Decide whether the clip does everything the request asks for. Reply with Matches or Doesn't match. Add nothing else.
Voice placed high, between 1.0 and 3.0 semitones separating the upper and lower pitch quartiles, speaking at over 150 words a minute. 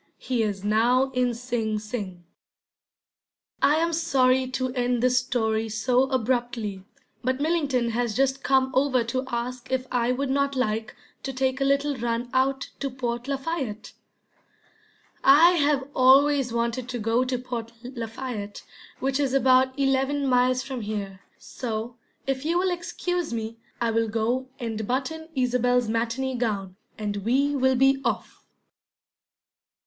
Doesn't match